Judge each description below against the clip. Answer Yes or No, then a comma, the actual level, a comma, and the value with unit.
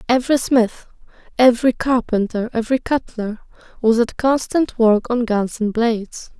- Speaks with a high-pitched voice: Yes, high, 235 Hz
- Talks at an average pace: No, slow, 130 wpm